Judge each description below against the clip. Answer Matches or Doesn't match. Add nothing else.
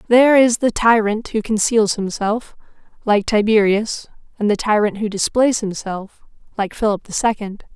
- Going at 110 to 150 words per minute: Matches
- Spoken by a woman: Matches